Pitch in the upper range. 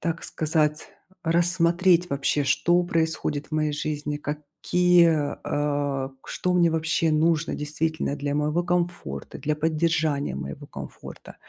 No: medium, 155 Hz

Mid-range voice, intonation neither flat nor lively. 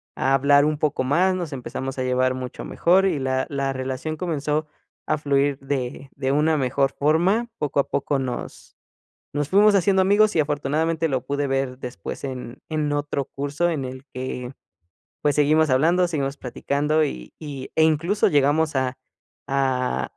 Yes: medium, 145 Hz; average, 3.0 semitones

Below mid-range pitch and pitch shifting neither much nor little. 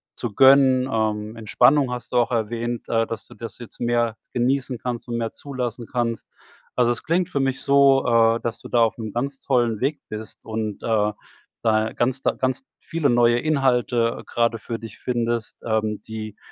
No: low, 120 Hz; narrow, 2.3 semitones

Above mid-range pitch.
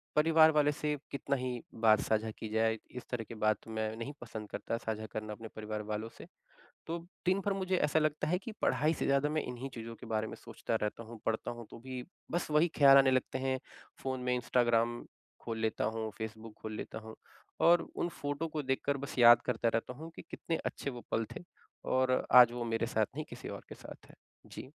No: low, 125 Hz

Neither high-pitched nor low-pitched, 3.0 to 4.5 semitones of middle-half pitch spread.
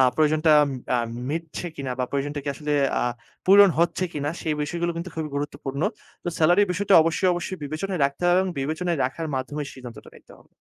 Yes: medium, 155 Hz; average, 3.4 semitones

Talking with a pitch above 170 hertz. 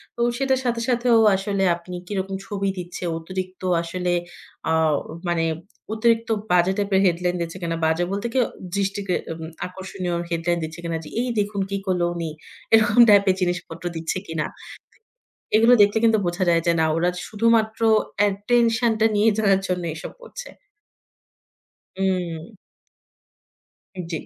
Yes: high, 190 Hz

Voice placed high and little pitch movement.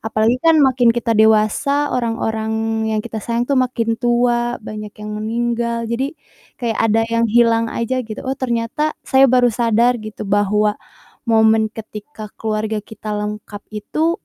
Yes: high, 230 Hz; narrow, 2.1 semitones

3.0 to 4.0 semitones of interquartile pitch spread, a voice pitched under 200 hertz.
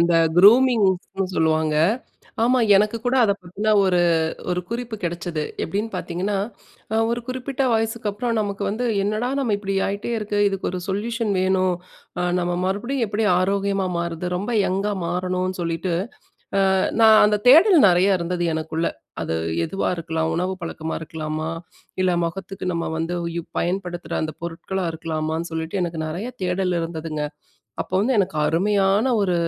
Yes: average, 3.5 semitones; high, 190 Hz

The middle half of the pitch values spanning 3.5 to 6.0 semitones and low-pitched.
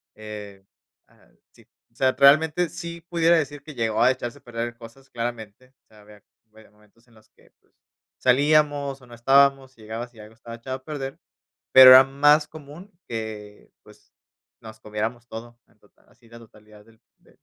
Yes: average, 3.9 semitones; low, 120 Hz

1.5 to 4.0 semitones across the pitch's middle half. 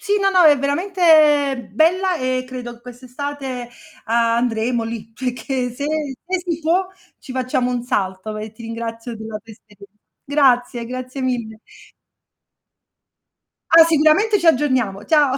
No: average, 4.5 semitones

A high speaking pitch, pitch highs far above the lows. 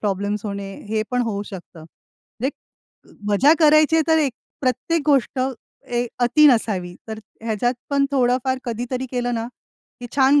No: high, 245 Hz; average, 4.2 semitones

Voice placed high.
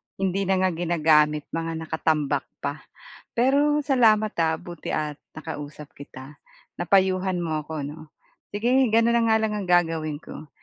No: medium, 170 Hz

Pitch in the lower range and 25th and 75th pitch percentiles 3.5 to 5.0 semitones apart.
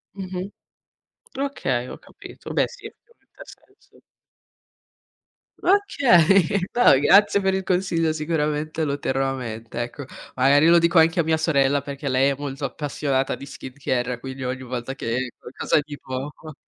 No: medium, 145 Hz; average, 4.3 semitones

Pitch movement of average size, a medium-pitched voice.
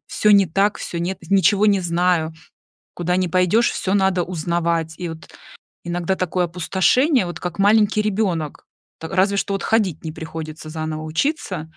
Yes: average, 3.3 semitones; medium, 180 Hz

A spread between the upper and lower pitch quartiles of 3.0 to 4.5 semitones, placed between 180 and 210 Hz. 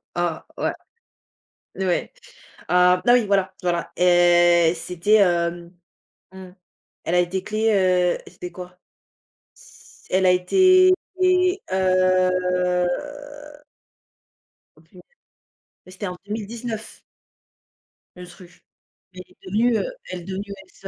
Yes: average, 3.4 semitones; medium, 185 Hz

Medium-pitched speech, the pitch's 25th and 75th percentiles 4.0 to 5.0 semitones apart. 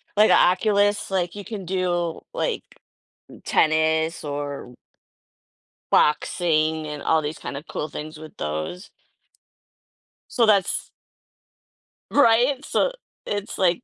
Yes: medium, 175 Hz; average, 4.7 semitones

